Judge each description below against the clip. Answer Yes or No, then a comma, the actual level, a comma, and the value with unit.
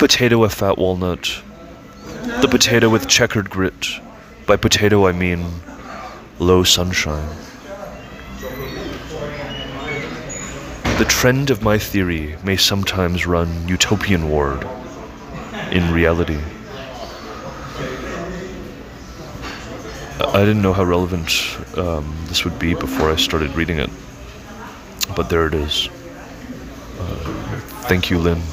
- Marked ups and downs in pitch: No, average, 3.2 semitones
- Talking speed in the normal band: No, slow, 105 wpm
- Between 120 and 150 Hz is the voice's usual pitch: No, very low, 90 Hz